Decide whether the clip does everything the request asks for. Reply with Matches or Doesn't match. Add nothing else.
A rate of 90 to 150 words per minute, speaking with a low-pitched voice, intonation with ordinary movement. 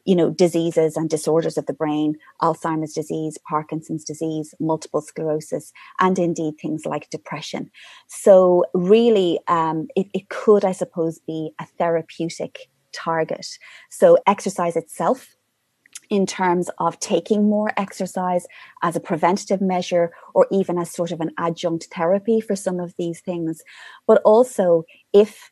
Doesn't match